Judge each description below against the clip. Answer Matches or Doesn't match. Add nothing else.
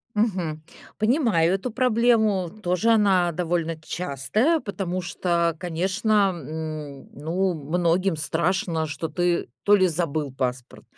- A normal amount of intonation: Matches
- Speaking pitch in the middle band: Matches